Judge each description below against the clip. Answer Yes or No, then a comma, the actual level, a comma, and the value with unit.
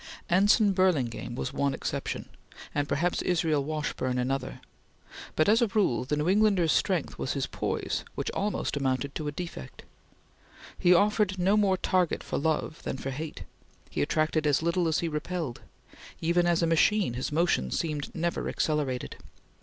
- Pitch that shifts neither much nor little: Yes, average, 4.4 semitones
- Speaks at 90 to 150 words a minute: No, average, 160 wpm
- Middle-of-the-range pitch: Yes, medium, 160 Hz